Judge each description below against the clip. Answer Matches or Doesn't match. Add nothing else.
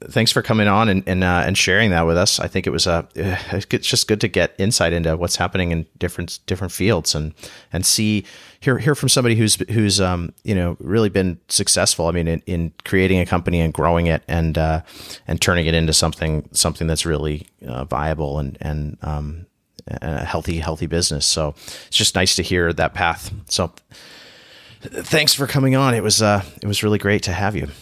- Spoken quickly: Matches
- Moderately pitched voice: Doesn't match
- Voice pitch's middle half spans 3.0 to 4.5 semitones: Matches